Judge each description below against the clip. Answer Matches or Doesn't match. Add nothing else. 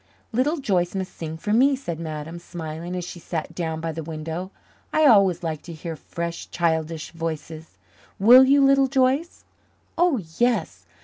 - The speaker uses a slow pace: Doesn't match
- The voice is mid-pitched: Matches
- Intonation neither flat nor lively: Doesn't match